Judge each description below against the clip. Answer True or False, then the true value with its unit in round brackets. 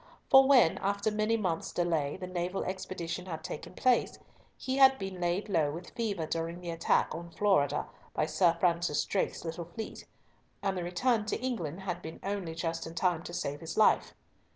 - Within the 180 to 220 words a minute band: True (185 wpm)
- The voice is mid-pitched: True (180 Hz)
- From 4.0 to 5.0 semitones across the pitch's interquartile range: False (3.5 semitones)